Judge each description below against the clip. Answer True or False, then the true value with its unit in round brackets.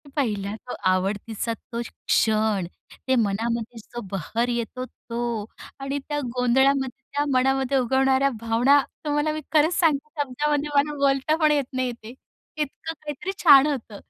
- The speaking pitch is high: True (260 Hz)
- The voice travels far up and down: False (3.8 semitones)